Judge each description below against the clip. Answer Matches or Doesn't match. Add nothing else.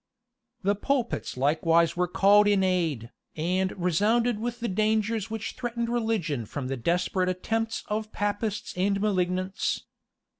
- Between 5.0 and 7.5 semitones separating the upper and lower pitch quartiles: Doesn't match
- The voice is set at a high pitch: Matches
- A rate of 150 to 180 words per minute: Doesn't match